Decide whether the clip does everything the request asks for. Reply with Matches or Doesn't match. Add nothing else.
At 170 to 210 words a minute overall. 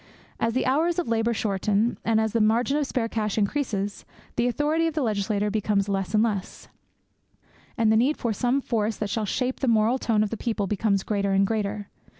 Matches